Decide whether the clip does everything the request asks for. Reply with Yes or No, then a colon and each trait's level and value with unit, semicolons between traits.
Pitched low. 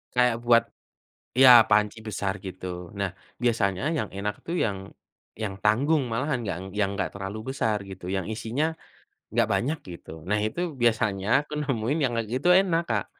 Yes: low, 110 Hz